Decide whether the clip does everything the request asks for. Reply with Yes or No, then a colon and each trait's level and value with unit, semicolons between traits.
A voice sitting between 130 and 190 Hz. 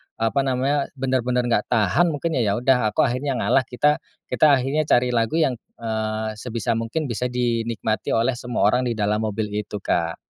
No: low, 120 Hz